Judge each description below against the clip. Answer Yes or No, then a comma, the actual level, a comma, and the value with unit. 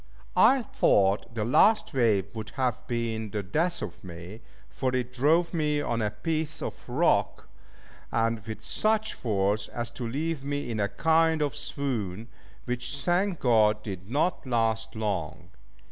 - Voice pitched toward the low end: Yes, low, 120 Hz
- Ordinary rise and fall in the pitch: No, wide, 5.8 semitones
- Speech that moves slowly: No, average, 155 wpm